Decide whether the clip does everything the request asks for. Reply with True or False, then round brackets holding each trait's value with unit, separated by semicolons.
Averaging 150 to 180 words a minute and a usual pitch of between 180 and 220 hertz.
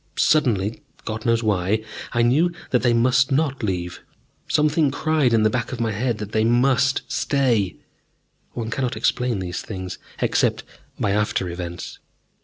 False (155 wpm; 115 Hz)